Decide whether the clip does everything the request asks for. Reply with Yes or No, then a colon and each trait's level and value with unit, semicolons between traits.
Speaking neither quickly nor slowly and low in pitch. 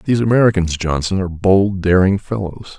Yes: average, 150 wpm; very low, 95 Hz